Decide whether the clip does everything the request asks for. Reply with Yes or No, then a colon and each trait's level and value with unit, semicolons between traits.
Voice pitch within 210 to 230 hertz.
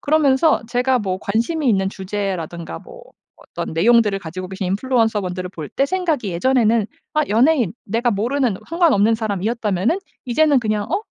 Yes: high, 225 Hz